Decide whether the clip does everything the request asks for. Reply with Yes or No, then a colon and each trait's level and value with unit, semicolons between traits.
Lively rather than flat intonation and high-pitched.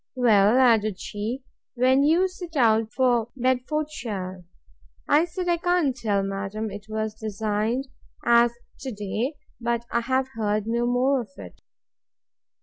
No: average, 3.8 semitones; high, 235 Hz